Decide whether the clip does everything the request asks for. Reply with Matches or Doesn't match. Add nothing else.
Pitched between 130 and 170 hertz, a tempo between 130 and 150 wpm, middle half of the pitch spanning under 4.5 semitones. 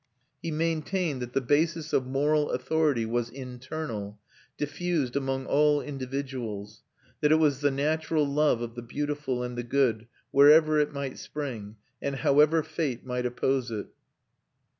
Matches